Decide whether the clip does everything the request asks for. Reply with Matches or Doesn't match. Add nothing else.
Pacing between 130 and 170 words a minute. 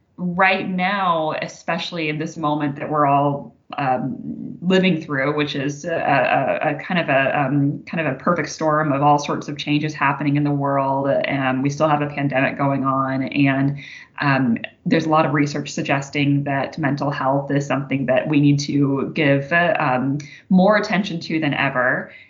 Doesn't match